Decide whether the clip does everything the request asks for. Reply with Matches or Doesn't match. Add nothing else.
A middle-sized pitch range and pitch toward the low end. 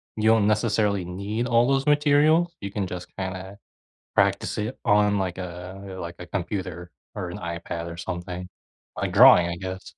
Matches